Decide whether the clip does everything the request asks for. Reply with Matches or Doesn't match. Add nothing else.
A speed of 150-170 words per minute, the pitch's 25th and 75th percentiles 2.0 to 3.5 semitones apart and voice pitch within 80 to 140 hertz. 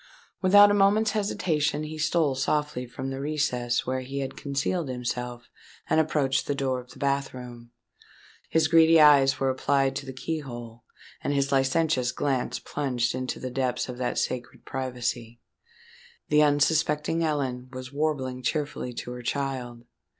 Matches